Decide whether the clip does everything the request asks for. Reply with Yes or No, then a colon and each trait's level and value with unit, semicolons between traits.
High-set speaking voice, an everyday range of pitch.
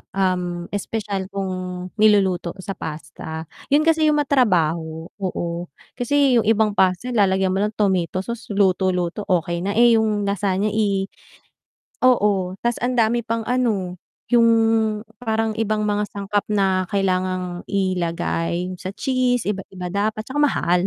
Yes: high, 200 Hz; average, 3.3 semitones